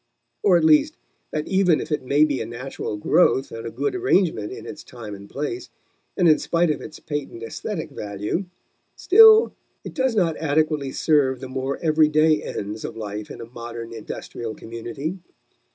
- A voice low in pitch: No, medium, 145 Hz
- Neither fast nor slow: Yes, average, 175 wpm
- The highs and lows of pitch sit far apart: Yes, wide, 5.9 semitones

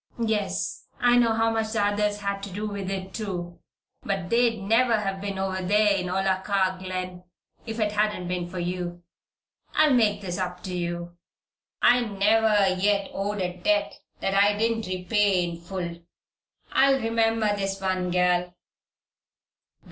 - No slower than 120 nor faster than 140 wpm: No, average, 155 wpm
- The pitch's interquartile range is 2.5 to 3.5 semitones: Yes, average, 2.9 semitones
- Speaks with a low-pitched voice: No, high, 195 Hz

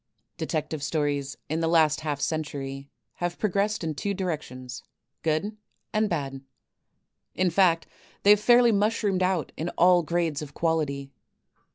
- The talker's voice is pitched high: No, medium, 165 Hz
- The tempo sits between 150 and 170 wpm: No, average, 140 wpm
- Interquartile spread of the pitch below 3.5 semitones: No, average, 4.4 semitones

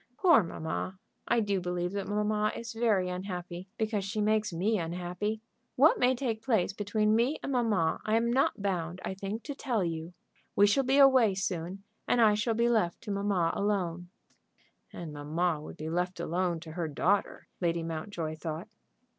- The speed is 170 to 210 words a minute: Yes, average, 180 wpm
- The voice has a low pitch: No, high, 195 Hz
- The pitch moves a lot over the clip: No, average, 4.0 semitones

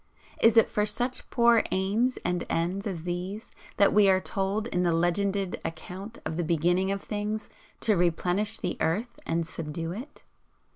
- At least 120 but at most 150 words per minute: No, average, 165 wpm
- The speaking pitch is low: No, high, 195 Hz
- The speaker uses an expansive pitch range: No, average, 3.3 semitones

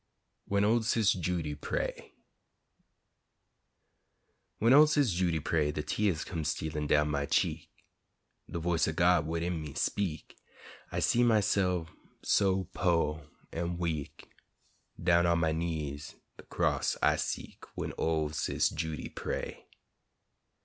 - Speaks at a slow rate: Yes, slow, 130 wpm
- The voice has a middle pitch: No, very low, 85 Hz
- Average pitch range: Yes, average, 3.3 semitones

